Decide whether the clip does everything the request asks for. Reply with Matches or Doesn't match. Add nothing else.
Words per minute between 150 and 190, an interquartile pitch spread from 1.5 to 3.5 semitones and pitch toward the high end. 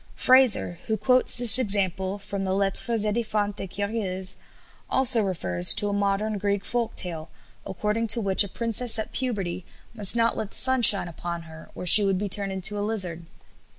Matches